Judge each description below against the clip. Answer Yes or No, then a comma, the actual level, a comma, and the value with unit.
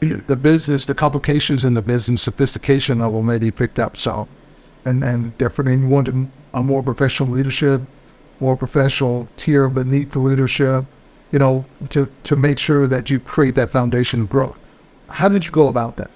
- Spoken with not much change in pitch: Yes, narrow, 1.9 semitones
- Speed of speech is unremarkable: Yes, average, 175 wpm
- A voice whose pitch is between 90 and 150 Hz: Yes, low, 135 Hz